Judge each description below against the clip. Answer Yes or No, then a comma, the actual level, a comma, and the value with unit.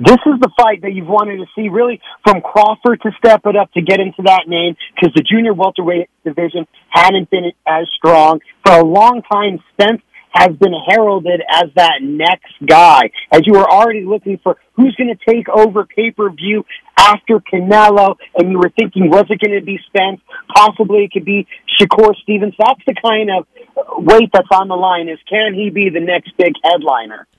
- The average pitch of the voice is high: Yes, high, 200 Hz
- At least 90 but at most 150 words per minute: No, average, 195 wpm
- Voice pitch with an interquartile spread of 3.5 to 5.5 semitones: No, average, 3.1 semitones